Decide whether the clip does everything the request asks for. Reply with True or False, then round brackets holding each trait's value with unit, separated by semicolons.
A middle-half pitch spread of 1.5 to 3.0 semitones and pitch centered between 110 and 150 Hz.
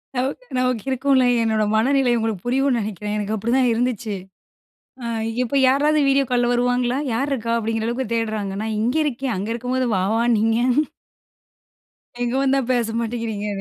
False (2.7 semitones; 240 Hz)